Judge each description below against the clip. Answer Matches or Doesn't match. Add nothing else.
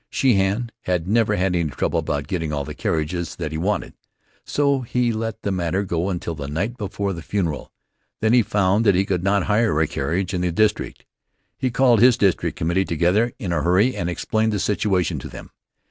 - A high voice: Doesn't match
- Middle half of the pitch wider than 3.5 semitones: Matches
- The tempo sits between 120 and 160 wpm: Doesn't match